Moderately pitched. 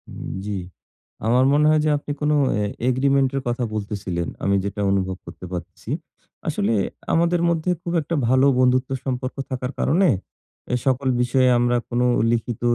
No: low, 125 Hz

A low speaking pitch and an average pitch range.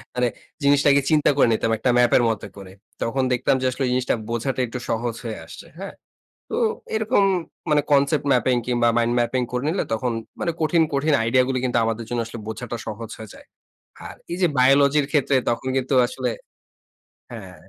Yes: low, 125 Hz; average, 3.2 semitones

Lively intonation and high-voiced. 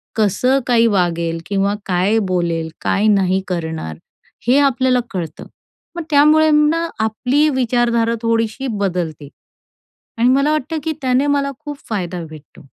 Yes: wide, 7.1 semitones; high, 225 Hz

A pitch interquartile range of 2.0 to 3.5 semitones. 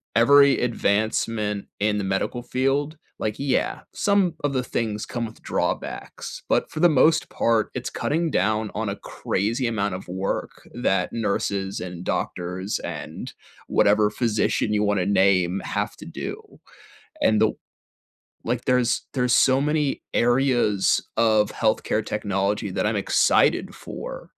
No: average, 4.1 semitones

